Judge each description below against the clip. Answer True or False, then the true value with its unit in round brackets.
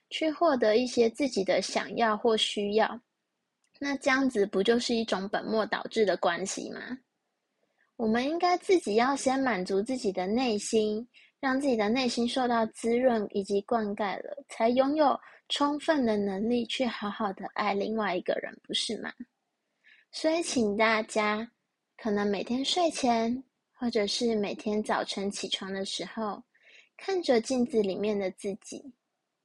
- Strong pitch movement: False (3.8 semitones)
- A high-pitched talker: True (230 Hz)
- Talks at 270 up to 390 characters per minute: False (230 characters per minute)